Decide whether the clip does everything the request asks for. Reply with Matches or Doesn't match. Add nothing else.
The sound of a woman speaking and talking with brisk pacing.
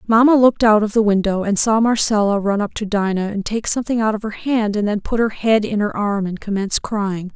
Matches